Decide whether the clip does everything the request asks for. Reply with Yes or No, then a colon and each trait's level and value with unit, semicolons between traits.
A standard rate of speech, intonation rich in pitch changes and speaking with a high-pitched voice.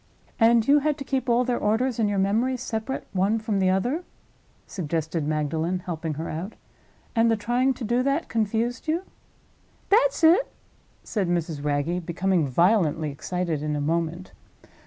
Yes: average, 160 wpm; wide, 6.7 semitones; high, 200 Hz